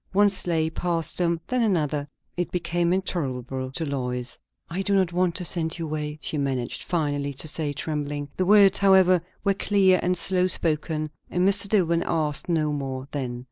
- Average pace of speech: Yes, average, 180 wpm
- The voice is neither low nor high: Yes, medium, 165 Hz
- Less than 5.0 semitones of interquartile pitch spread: Yes, average, 4.1 semitones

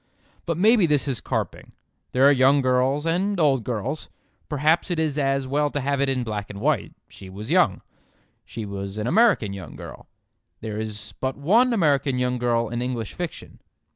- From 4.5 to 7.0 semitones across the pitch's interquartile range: Yes, average, 4.8 semitones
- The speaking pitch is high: No, low, 135 Hz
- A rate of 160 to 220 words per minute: Yes, average, 185 wpm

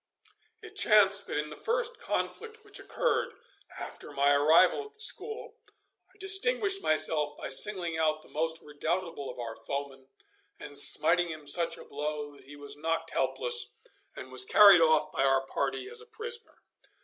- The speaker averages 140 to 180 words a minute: Yes, average, 170 wpm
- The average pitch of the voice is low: No, medium, 165 Hz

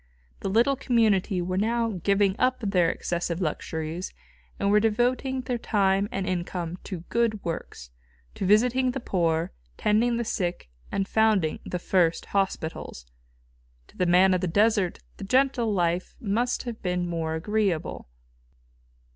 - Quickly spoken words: No, average, 145 wpm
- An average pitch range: Yes, average, 4.4 semitones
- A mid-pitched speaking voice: No, high, 195 Hz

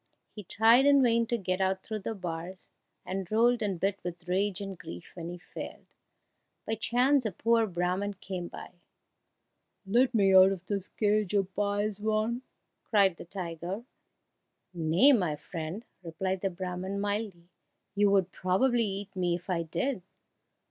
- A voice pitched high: Yes, high, 195 Hz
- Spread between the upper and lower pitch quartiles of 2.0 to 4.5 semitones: Yes, average, 3.2 semitones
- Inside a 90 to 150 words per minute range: No, average, 160 wpm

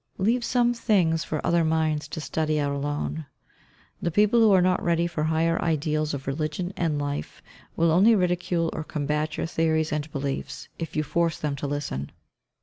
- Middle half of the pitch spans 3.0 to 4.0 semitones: No, narrow, 2.4 semitones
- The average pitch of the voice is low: No, medium, 160 Hz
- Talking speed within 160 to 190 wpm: Yes, average, 180 wpm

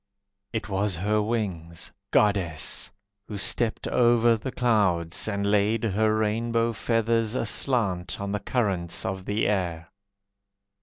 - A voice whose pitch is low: Yes, low, 105 Hz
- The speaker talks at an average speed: No, slow, 120 wpm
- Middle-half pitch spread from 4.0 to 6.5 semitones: No, average, 3.2 semitones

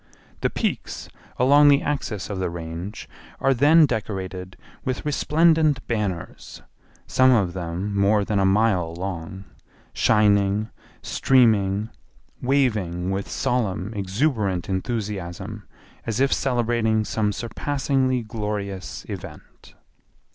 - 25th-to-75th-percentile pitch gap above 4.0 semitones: Yes, average, 4.8 semitones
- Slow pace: Yes, slow, 105 wpm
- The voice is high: No, low, 105 Hz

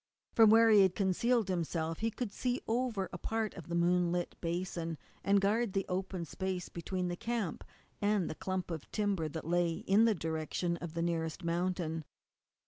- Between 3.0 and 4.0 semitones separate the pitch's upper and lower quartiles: Yes, average, 3.4 semitones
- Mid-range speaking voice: Yes, medium, 180 Hz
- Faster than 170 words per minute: Yes, average, 180 wpm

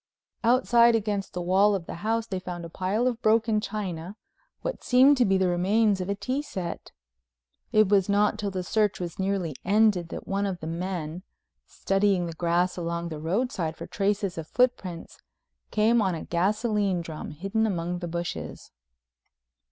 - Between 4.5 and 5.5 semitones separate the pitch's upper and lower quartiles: No, average, 3.6 semitones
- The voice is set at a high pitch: Yes, high, 195 Hz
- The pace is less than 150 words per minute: No, average, 175 wpm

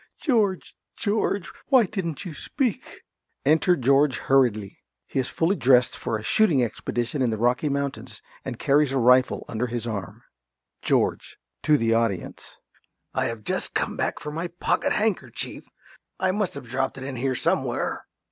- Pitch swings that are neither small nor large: No, wide, 6.0 semitones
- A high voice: No, low, 135 Hz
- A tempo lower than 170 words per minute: Yes, average, 160 wpm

